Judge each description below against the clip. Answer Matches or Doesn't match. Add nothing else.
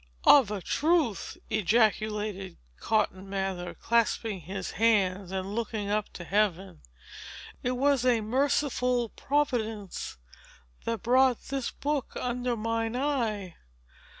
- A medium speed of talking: Doesn't match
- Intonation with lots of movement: Doesn't match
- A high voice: Matches